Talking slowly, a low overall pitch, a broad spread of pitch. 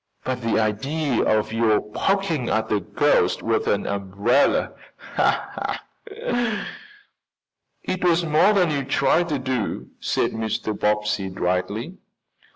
Yes: slow, 115 wpm; low, 125 Hz; wide, 8.5 semitones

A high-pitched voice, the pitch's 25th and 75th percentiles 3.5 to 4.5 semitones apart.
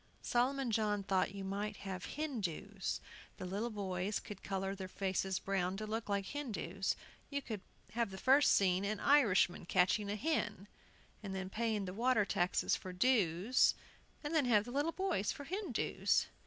Yes: high, 205 Hz; average, 4.2 semitones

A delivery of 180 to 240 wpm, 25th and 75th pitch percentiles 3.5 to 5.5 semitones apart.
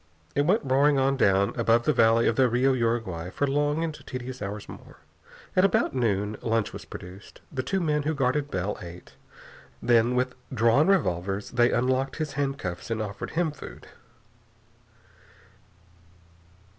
No: average, 155 wpm; average, 4.8 semitones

